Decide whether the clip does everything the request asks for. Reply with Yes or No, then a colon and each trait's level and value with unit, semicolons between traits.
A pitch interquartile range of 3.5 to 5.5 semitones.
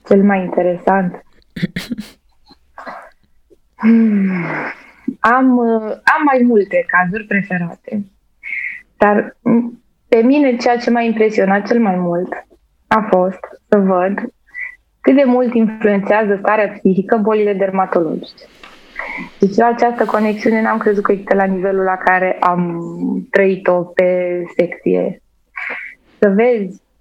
Yes: average, 3.9 semitones